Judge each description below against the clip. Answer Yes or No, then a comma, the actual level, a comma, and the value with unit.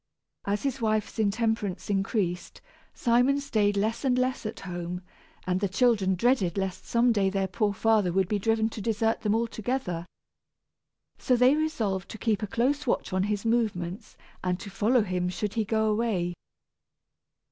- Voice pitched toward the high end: Yes, high, 215 Hz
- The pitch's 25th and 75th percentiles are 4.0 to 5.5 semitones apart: No, average, 3.4 semitones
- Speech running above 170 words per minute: No, average, 165 wpm